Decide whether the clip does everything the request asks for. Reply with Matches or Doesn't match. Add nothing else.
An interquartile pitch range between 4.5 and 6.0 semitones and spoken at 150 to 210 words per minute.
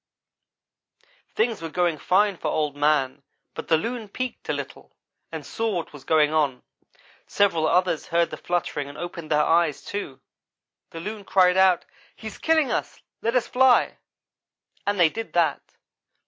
Matches